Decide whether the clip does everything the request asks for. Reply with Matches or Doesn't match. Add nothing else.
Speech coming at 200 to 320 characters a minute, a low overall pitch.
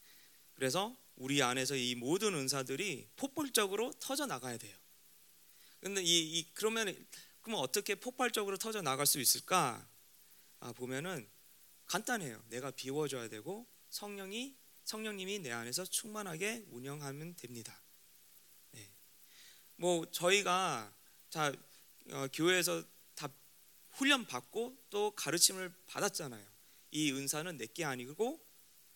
Doesn't match